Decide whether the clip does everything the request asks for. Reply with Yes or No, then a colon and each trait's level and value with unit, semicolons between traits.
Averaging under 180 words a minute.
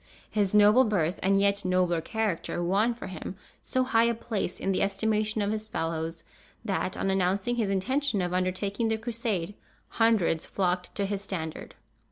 Yes: average, 170 wpm